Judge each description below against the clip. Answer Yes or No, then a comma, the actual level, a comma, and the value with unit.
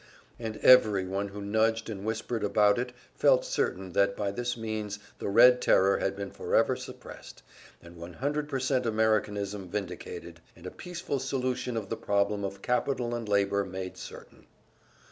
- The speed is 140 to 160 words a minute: Yes, average, 155 wpm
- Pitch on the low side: Yes, low, 105 Hz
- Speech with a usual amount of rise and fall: Yes, average, 3.6 semitones